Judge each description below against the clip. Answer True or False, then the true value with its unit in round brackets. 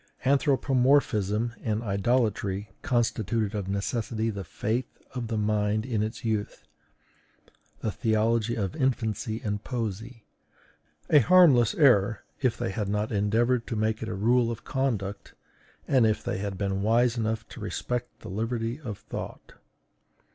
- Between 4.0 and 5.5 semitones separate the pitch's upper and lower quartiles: False (2.5 semitones)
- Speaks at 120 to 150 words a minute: True (140 wpm)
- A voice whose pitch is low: True (110 Hz)